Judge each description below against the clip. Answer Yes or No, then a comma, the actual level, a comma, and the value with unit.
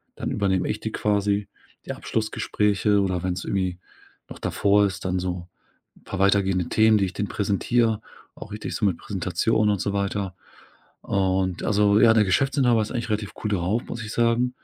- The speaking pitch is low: Yes, low, 100 Hz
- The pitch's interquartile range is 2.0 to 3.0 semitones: Yes, narrow, 2.4 semitones